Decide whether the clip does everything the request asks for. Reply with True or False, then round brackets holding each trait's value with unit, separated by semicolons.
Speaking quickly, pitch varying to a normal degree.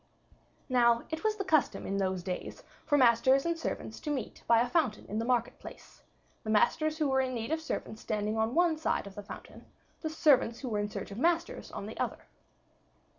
False (215 wpm; 6.4 semitones)